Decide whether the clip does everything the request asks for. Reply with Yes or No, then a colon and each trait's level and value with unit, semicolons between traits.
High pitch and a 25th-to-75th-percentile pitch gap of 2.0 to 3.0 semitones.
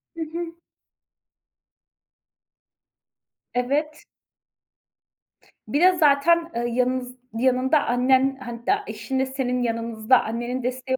Yes: very high, 260 Hz; average, 2.7 semitones